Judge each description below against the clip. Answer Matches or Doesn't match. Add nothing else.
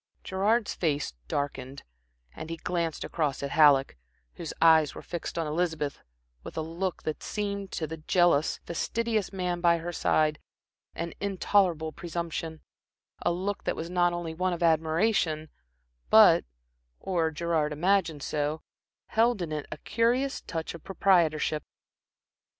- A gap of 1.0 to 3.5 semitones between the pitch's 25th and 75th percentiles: Matches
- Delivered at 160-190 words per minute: Doesn't match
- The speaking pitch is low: Doesn't match